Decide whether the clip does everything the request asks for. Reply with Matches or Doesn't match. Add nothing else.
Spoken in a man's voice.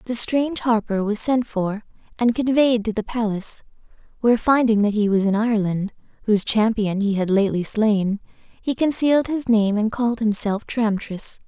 Doesn't match